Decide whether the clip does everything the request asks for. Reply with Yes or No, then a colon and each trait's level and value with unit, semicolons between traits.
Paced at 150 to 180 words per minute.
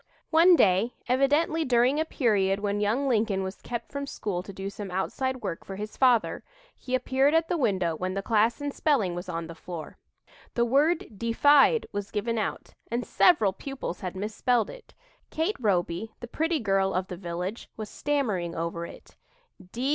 Yes: average, 175 wpm